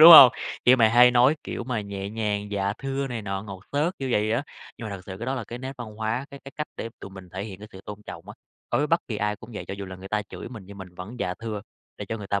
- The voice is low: Yes, low, 110 Hz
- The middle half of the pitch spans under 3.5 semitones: No, average, 3.9 semitones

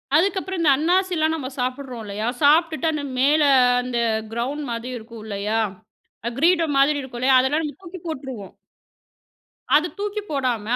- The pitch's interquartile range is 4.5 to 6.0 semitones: Yes, average, 5.0 semitones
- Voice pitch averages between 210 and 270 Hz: No, very high, 280 Hz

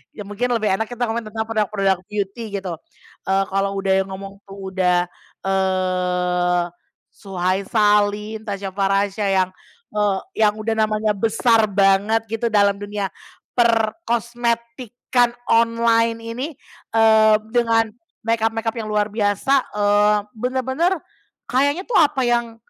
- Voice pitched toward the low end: No, high, 215 Hz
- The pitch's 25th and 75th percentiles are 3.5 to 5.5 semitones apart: No, average, 2.8 semitones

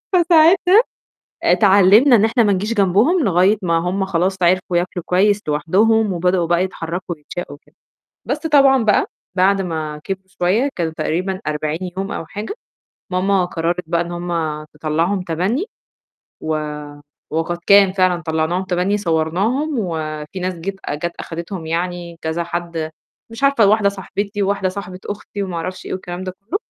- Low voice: No, medium, 185 Hz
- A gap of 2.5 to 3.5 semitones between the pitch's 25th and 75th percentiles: Yes, average, 3.1 semitones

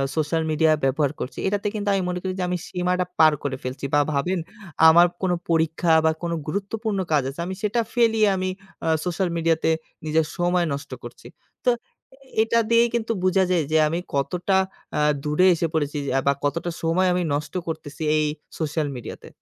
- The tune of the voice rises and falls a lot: No, average, 3.4 semitones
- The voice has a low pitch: No, medium, 170 Hz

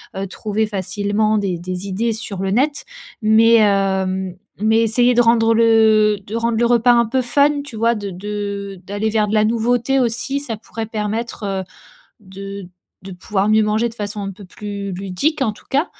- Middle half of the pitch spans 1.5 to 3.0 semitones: Yes, average, 2.7 semitones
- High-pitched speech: Yes, high, 215 Hz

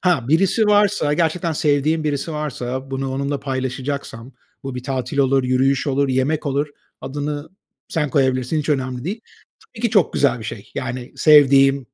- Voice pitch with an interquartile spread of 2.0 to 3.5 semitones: Yes, narrow, 2.6 semitones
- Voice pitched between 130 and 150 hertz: Yes, medium, 140 Hz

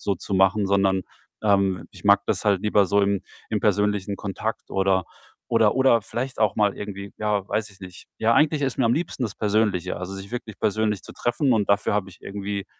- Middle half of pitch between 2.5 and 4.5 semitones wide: No, narrow, 2.0 semitones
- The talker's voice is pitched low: Yes, low, 100 Hz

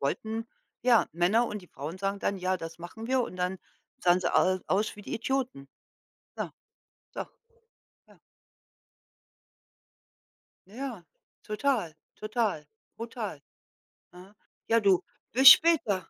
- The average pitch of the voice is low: No, high, 200 Hz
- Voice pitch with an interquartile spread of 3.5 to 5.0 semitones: Yes, average, 4.3 semitones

